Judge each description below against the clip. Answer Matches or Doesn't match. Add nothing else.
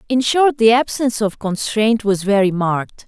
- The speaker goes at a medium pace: Matches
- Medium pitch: Doesn't match